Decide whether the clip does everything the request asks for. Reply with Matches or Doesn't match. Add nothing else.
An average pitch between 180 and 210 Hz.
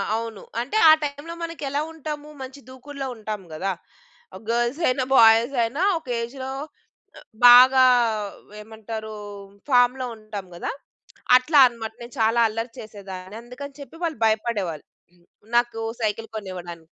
Doesn't match